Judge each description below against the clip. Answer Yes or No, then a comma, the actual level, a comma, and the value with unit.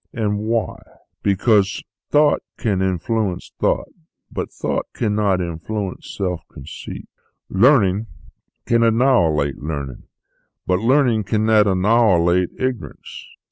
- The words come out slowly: Yes, slow, 100 wpm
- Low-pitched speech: Yes, low, 105 Hz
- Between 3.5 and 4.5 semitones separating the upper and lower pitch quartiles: Yes, average, 3.8 semitones